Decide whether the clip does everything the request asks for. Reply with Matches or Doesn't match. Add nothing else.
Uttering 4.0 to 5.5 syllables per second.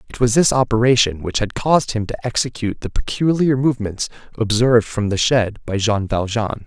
Doesn't match